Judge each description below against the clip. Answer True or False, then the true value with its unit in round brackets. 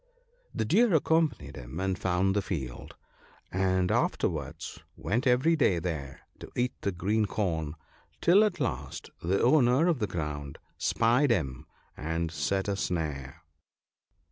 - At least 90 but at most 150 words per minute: True (140 wpm)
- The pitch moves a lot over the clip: True (7.2 semitones)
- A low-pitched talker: True (95 Hz)